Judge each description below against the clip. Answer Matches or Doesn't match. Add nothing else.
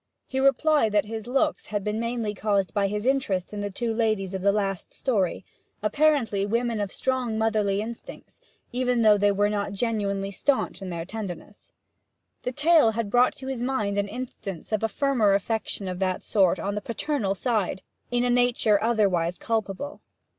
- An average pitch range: Matches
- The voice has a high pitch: Matches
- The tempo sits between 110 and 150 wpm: Doesn't match